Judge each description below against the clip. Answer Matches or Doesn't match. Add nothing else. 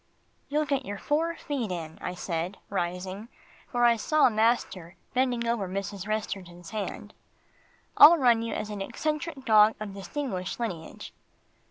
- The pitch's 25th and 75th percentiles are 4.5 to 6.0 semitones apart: Matches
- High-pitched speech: Matches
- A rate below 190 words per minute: Matches